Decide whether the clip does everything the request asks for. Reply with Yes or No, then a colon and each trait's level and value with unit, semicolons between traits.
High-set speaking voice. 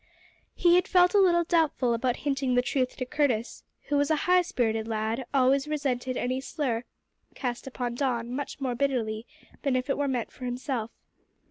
Yes: very high, 260 Hz